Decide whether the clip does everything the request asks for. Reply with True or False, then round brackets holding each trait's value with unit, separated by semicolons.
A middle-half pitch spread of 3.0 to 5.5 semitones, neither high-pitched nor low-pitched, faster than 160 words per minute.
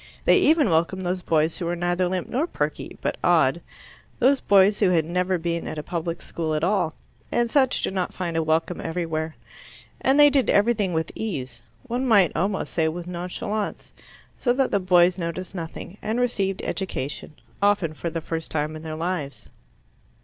True (3.8 semitones; 180 Hz; 185 wpm)